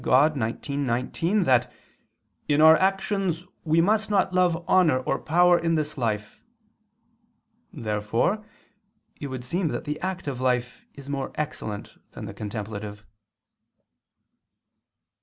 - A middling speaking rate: No, slow, 120 wpm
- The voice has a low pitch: No, medium, 145 Hz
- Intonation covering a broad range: Yes, wide, 6.2 semitones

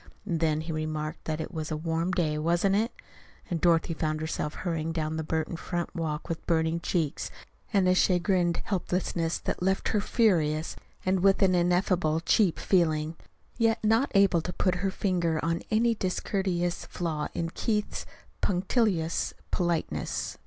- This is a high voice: No, medium, 170 Hz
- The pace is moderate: Yes, average, 160 wpm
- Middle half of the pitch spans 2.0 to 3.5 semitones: Yes, average, 2.9 semitones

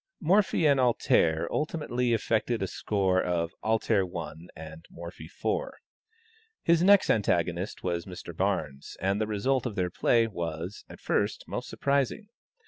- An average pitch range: No, wide, 6.4 semitones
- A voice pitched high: No, low, 100 Hz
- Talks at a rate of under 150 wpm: Yes, average, 140 wpm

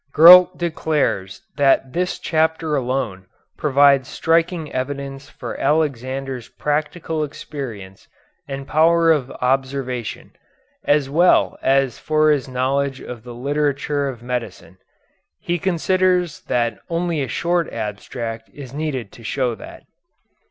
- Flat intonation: No, average, 3.8 semitones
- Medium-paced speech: No, slow, 115 wpm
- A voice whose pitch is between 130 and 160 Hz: Yes, medium, 140 Hz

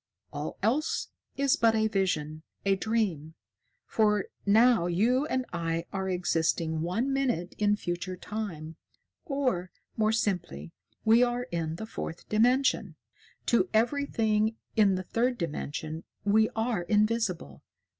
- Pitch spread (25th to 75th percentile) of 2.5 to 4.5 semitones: No, average, 5.0 semitones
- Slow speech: Yes, slow, 125 wpm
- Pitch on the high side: Yes, high, 210 Hz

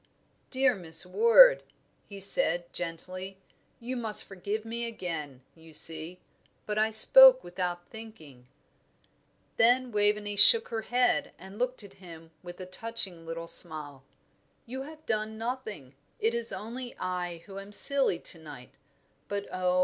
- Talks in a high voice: Yes, high, 200 Hz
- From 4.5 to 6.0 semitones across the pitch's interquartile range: Yes, average, 5.1 semitones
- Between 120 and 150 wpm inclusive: Yes, average, 140 wpm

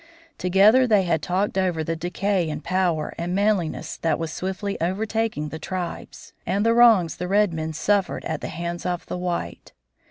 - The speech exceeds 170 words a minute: Yes, average, 180 wpm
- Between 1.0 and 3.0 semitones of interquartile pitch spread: No, average, 3.4 semitones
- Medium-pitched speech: Yes, medium, 180 Hz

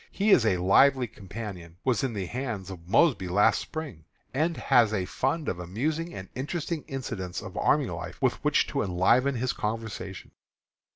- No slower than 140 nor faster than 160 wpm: No, average, 170 wpm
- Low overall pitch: Yes, low, 115 Hz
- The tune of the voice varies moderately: No, wide, 6.3 semitones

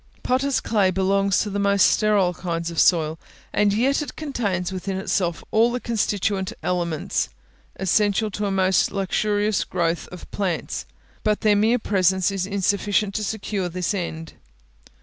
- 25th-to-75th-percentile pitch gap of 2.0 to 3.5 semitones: Yes, narrow, 2.6 semitones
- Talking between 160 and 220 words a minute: No, average, 150 wpm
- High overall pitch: Yes, high, 195 Hz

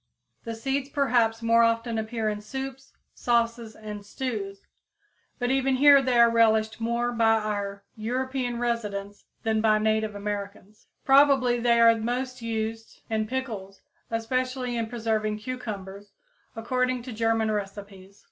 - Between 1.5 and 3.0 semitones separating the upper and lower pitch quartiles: Yes, narrow, 2.5 semitones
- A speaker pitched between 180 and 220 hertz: No, high, 230 Hz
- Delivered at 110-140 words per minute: Yes, slow, 135 wpm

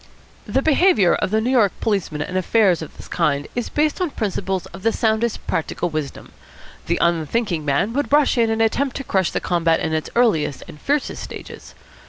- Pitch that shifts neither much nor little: No, wide, 6.4 semitones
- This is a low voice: No, high, 205 Hz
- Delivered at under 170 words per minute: No, average, 195 wpm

